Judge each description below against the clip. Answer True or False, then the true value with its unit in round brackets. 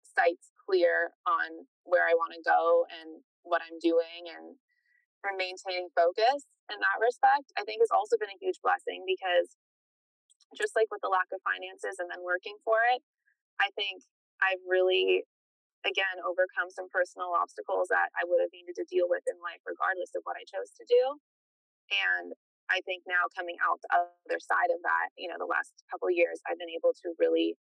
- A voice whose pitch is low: False (215 Hz)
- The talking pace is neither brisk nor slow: True (195 wpm)